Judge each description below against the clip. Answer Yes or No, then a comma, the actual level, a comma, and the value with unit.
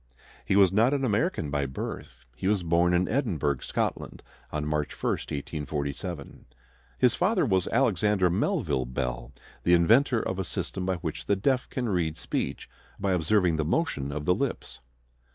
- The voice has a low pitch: Yes, very low, 90 Hz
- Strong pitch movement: Yes, wide, 5.9 semitones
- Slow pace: No, average, 165 wpm